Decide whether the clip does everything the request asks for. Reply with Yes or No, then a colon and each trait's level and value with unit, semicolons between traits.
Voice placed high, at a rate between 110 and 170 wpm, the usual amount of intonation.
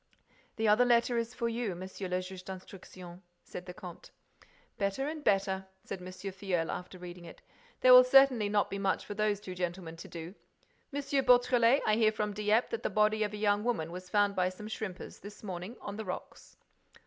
No: high, 205 Hz; average, 200 wpm; average, 3.6 semitones